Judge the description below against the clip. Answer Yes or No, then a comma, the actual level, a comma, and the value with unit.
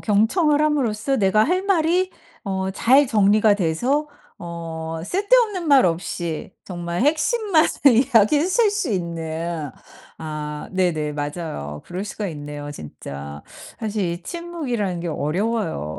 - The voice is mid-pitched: No, high, 200 Hz